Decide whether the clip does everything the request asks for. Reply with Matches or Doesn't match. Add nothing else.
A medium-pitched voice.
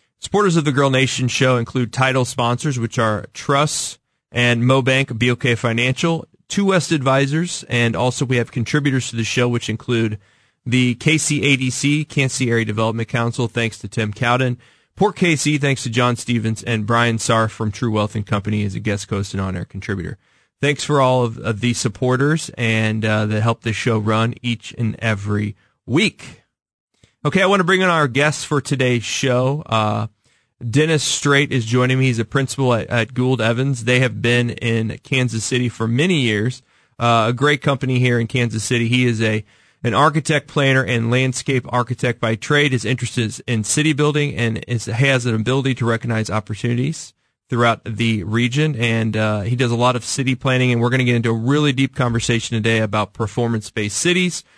Doesn't match